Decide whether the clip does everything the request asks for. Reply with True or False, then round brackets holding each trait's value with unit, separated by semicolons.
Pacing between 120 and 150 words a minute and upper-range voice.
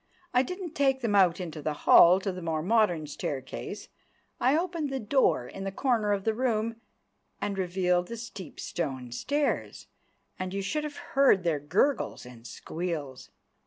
False (165 wpm; 195 Hz)